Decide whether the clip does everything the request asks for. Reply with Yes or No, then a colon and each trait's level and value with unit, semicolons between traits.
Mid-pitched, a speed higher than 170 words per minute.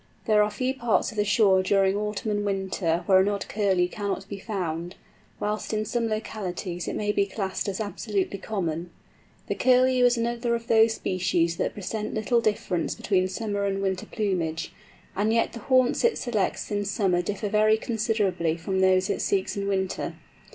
No: high, 205 Hz; average, 180 wpm